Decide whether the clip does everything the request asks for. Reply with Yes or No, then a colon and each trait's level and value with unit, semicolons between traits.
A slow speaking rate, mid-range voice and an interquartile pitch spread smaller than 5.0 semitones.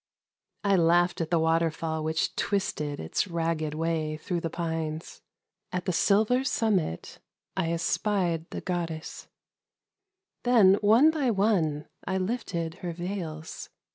Yes: slow, 120 wpm; medium, 170 Hz; average, 3.5 semitones